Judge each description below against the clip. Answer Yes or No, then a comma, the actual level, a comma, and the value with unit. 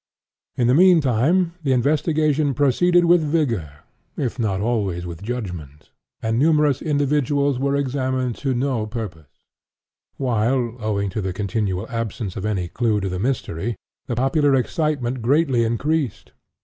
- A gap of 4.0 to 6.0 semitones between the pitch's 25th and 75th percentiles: Yes, average, 5.1 semitones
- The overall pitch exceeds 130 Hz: No, low, 125 Hz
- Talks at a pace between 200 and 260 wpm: No, average, 140 wpm